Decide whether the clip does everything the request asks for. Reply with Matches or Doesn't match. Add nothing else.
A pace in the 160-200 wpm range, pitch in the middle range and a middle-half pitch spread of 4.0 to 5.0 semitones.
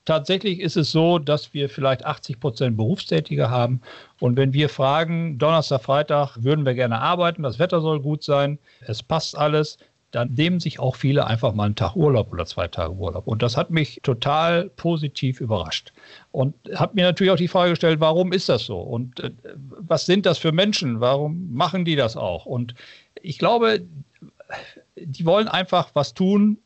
Matches